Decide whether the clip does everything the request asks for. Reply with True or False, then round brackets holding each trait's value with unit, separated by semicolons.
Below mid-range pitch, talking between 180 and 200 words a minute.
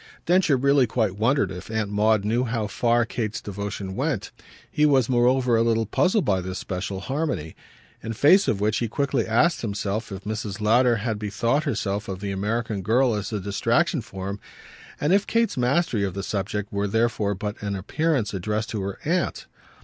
True (110 Hz; 190 wpm)